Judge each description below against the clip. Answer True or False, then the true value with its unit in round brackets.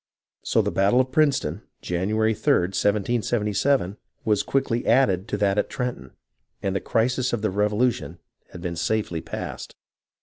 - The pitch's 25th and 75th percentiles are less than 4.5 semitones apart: True (3.8 semitones)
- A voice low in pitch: True (105 Hz)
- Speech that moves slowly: False (145 wpm)